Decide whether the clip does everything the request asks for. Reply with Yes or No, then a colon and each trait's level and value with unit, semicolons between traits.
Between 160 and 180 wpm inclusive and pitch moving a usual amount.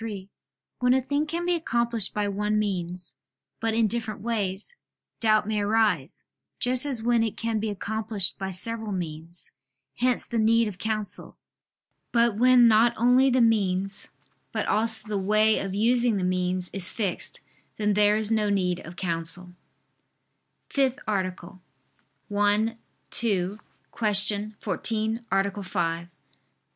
No: average, 140 wpm; average, 3.1 semitones